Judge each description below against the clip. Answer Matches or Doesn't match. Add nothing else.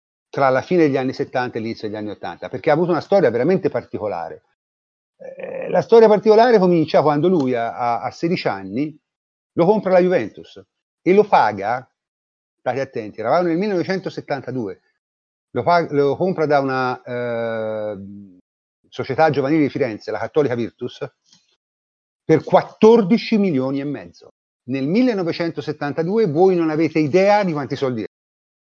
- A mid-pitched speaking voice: Matches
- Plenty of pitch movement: Matches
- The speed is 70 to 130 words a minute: Doesn't match